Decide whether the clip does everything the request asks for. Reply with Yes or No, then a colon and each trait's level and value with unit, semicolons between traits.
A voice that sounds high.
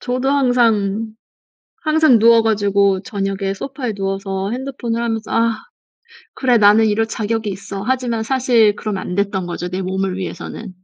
Yes: high, 220 Hz